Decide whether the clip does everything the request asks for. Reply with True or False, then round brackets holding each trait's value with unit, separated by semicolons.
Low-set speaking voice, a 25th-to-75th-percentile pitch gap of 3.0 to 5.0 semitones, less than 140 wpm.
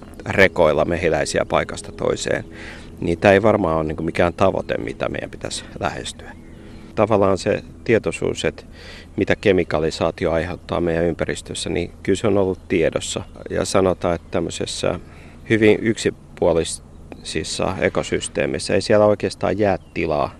True (85 Hz; 3.4 semitones; 125 wpm)